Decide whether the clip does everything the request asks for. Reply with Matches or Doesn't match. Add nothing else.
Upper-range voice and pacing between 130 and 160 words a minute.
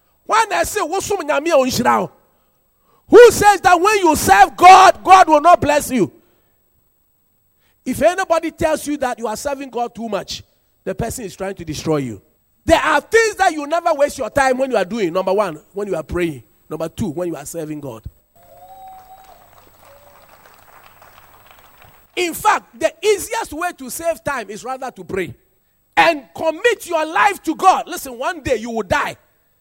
Doesn't match